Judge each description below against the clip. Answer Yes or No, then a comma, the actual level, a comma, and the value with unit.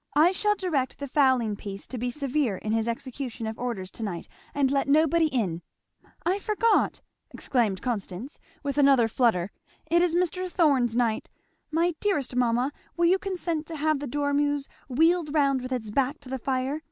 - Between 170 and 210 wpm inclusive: Yes, average, 175 wpm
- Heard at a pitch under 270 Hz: No, very high, 275 Hz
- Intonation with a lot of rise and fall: No, average, 4.8 semitones